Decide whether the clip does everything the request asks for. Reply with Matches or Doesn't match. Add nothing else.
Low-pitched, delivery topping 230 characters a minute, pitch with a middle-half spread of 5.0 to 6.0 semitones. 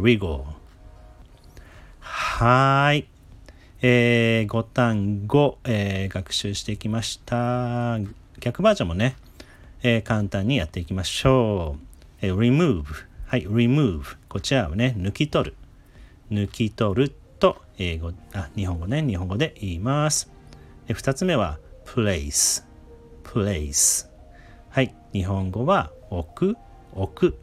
Doesn't match